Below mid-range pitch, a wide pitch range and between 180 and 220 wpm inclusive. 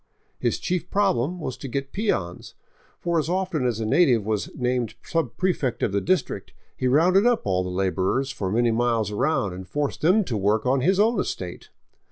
Yes: low, 130 Hz; wide, 8.6 semitones; average, 190 wpm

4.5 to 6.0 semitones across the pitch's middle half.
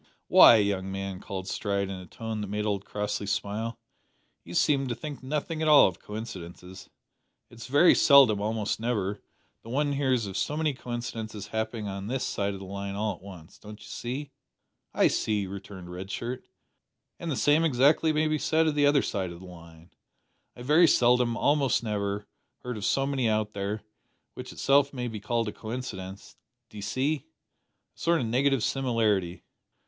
Yes: average, 5.2 semitones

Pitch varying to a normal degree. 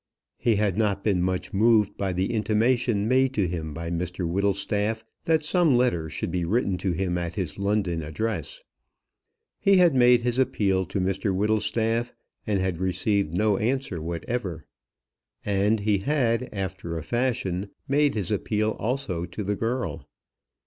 Yes: average, 4.3 semitones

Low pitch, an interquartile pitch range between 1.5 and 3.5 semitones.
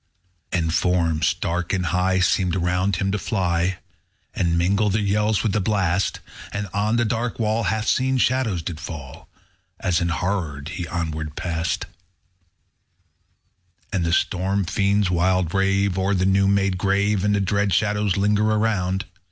Yes: very low, 95 Hz; average, 2.8 semitones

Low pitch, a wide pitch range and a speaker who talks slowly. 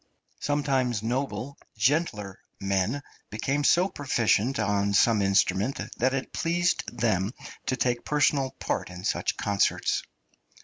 Yes: low, 120 Hz; wide, 5.8 semitones; slow, 120 wpm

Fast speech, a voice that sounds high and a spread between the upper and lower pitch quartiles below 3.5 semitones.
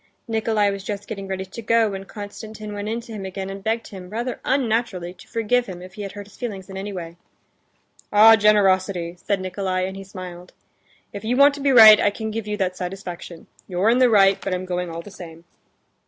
Yes: fast, 225 wpm; high, 200 Hz; average, 2.9 semitones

